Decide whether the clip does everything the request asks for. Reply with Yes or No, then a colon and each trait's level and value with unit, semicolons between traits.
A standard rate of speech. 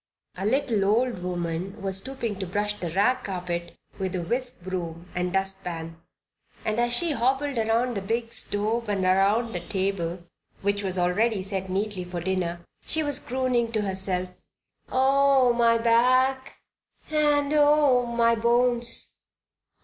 Yes: average, 145 wpm